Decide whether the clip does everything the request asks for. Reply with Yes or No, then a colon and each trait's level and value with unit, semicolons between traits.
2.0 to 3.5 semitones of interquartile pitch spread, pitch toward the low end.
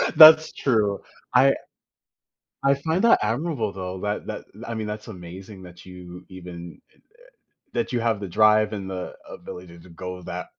No: average, 4.0 semitones; low, 100 Hz